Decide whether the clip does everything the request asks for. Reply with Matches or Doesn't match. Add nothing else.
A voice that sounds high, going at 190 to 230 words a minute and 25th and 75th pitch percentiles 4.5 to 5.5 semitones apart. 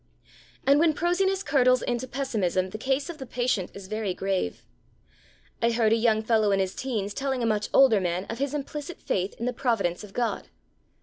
Matches